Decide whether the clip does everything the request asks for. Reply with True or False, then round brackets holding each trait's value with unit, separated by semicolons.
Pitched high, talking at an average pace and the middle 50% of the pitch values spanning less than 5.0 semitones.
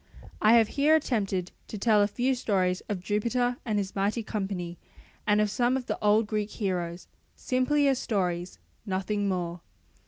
True (210 Hz; 165 wpm; 4.1 semitones)